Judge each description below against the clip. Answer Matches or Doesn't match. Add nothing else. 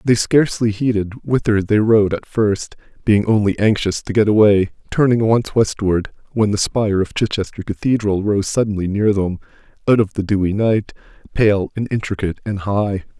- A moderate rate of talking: Matches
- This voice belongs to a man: Matches